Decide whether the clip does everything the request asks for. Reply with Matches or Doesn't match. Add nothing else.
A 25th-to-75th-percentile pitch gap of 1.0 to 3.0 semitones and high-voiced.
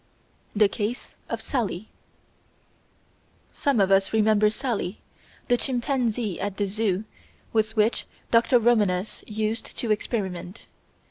Matches